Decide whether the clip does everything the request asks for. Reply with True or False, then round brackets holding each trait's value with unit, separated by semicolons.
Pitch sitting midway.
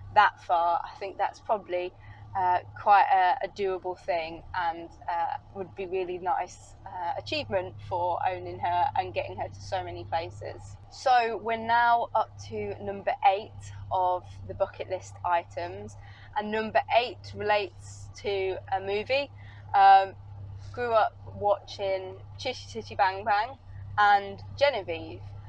True (175 Hz)